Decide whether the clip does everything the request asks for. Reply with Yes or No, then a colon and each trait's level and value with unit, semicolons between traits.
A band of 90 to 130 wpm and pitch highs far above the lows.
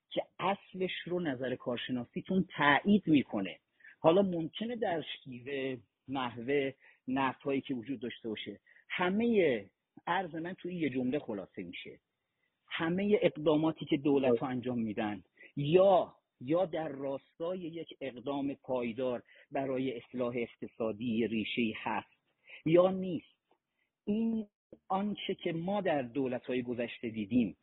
Yes: average, 115 wpm; wide, 6.1 semitones